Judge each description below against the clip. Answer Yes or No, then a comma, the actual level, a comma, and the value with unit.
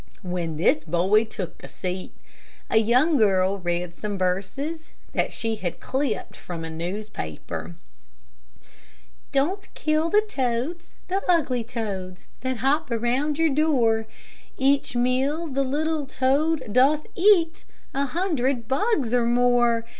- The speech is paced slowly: Yes, slow, 130 wpm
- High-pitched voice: Yes, very high, 250 Hz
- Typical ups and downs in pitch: No, wide, 6.6 semitones